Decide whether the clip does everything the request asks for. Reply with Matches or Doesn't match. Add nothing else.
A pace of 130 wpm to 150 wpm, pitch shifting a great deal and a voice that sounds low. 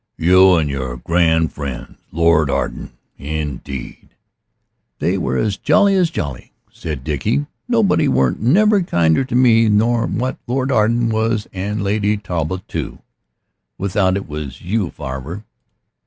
Matches